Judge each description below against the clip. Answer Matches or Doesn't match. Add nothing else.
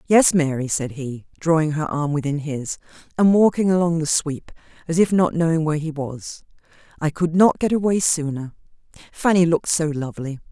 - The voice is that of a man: Doesn't match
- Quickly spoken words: Doesn't match